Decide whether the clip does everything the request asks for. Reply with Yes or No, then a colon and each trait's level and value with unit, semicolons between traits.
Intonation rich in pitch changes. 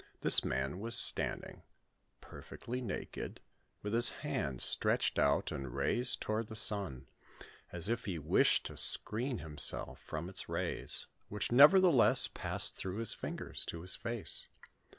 Yes: wide, 6.1 semitones